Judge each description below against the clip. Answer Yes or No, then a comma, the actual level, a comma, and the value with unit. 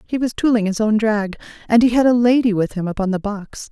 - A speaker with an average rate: No, fast, 260 wpm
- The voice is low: No, high, 220 Hz